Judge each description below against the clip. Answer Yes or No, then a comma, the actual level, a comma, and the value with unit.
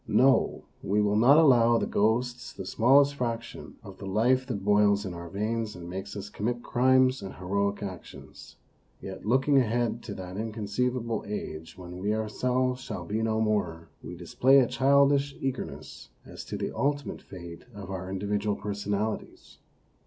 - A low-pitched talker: Yes, low, 110 Hz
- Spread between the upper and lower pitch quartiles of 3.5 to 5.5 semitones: Yes, average, 4.2 semitones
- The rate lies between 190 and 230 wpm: No, average, 165 wpm